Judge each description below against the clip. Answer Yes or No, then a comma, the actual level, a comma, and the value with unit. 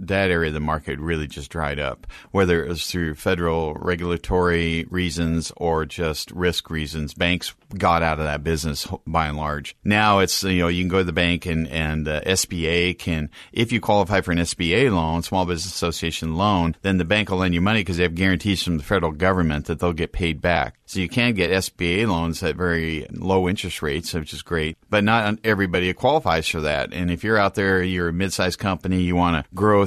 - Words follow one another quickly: Yes, fast, 220 wpm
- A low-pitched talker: Yes, very low, 85 Hz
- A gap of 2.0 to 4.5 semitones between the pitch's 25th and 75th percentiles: Yes, average, 2.7 semitones